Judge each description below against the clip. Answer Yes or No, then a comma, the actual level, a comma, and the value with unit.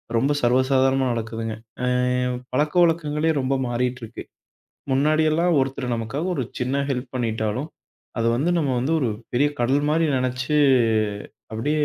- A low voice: Yes, low, 130 Hz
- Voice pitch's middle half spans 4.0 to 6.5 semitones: No, average, 3.2 semitones